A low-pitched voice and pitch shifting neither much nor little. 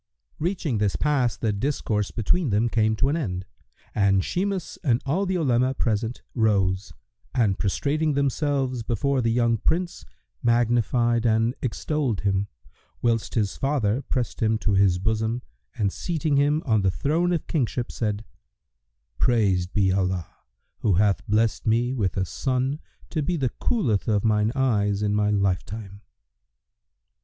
Yes: low, 115 Hz; average, 4.9 semitones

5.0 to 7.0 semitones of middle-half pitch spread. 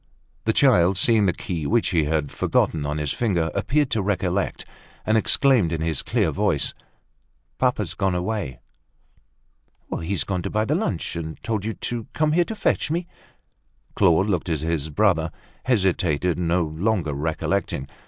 Yes: average, 5.3 semitones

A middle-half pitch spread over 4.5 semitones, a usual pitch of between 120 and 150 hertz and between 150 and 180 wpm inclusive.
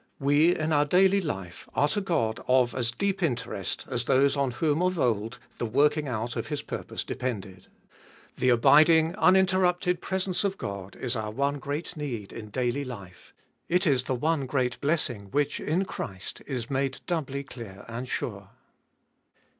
Yes: wide, 5.4 semitones; medium, 140 Hz; average, 165 wpm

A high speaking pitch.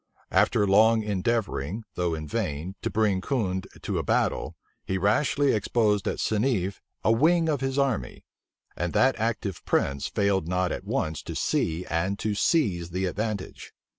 No: low, 100 Hz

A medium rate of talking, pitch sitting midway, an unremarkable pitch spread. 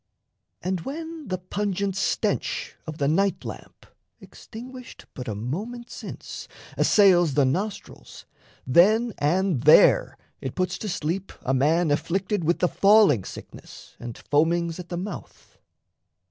No: slow, 130 wpm; medium, 180 Hz; average, 5.0 semitones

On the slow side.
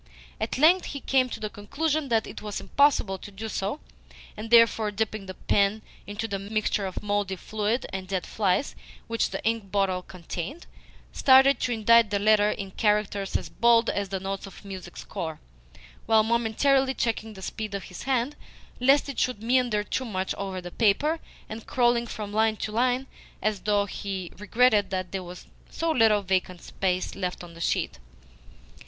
No: average, 180 wpm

